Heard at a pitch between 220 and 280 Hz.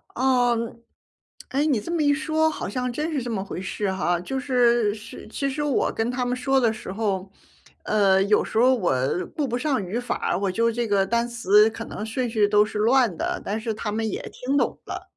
Yes: high, 235 Hz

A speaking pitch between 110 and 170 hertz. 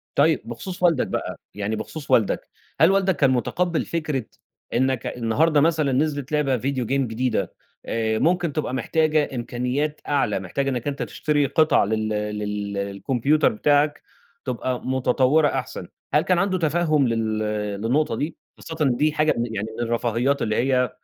Yes: low, 135 Hz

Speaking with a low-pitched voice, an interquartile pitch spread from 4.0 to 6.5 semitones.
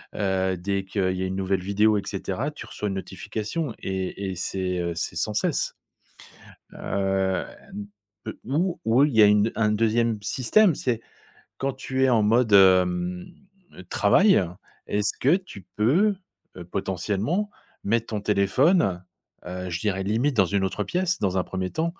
Yes: low, 105 Hz; average, 4.6 semitones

